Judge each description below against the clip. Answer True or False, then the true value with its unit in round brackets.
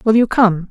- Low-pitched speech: False (210 Hz)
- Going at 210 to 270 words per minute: True (255 wpm)